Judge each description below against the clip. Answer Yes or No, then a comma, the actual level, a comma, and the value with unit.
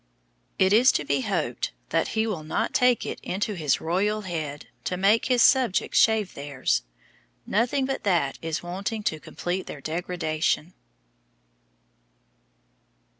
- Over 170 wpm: No, slow, 135 wpm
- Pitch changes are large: Yes, wide, 5.7 semitones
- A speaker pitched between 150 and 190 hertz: Yes, medium, 185 Hz